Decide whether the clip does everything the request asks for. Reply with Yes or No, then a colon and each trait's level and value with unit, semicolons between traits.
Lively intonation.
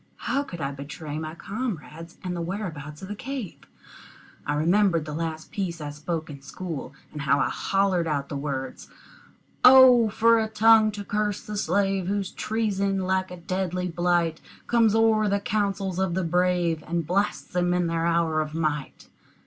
No: average, 4.2 semitones